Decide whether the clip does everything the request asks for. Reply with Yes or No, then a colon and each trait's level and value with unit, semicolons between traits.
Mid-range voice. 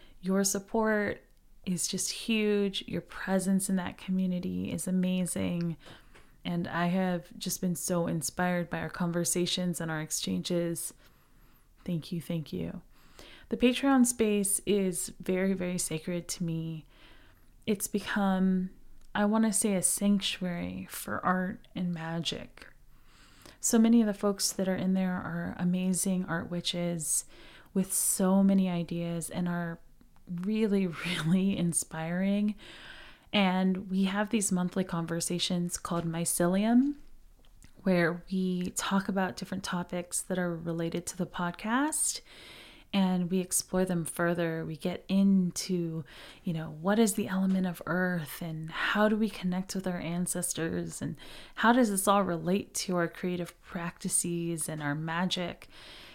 Yes: medium, 180 Hz